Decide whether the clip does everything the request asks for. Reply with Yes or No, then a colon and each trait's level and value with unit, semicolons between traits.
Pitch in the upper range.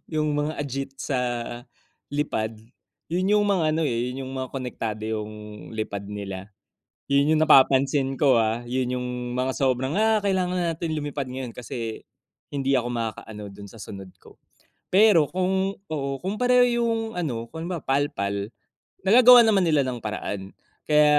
No: low, 135 Hz